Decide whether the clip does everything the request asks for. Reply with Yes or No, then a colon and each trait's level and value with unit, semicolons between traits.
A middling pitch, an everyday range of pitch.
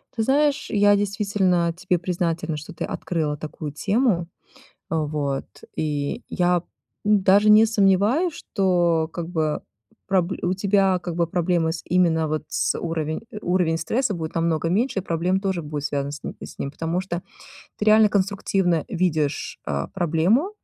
Yes: medium, 175 Hz; average, 3.6 semitones